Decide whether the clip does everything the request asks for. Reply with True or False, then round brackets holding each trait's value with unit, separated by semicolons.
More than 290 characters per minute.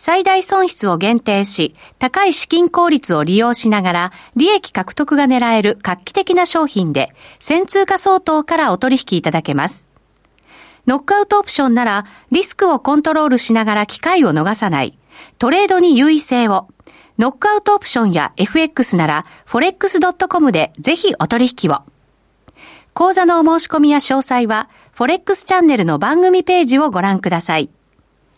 True (340 characters per minute)